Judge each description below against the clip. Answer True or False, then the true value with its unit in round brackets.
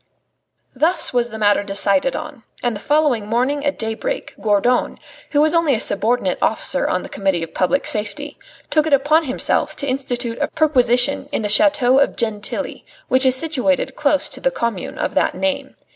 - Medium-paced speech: True (180 wpm)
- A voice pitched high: True (260 Hz)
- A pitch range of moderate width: True (4.7 semitones)